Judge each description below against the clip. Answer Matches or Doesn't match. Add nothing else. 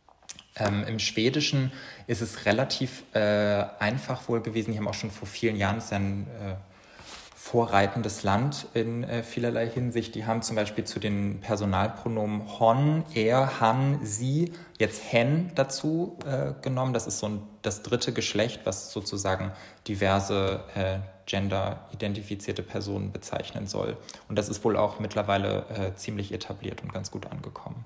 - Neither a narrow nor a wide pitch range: Matches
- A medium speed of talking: Matches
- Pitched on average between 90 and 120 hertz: Matches